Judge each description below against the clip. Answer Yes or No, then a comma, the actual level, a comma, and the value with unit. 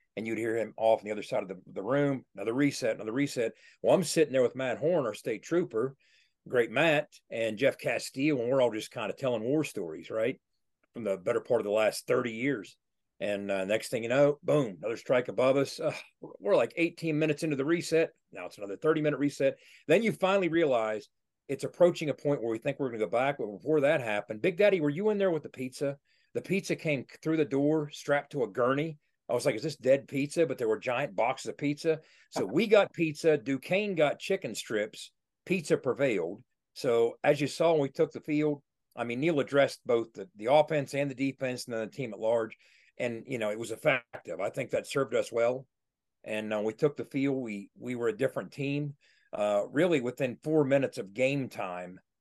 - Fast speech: Yes, fast, 225 wpm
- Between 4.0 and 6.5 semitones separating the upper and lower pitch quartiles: Yes, average, 4.5 semitones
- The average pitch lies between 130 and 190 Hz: Yes, medium, 140 Hz